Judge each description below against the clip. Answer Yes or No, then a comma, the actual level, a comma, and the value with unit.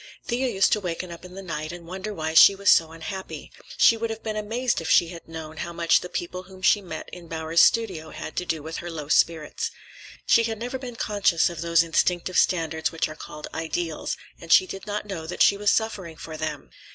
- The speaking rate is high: Yes, fast, 230 wpm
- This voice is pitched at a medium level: Yes, medium, 175 Hz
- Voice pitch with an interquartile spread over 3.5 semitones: Yes, average, 3.9 semitones